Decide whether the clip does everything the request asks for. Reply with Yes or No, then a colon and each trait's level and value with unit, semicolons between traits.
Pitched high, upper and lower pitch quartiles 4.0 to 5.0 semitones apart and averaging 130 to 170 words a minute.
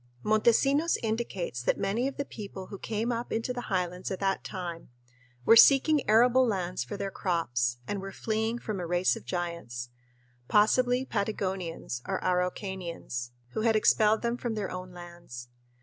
Yes: high, 195 Hz; average, 4.4 semitones; average, 165 wpm